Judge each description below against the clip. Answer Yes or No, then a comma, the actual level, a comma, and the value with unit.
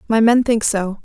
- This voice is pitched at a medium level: No, high, 220 Hz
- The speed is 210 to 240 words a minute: Yes, fast, 230 wpm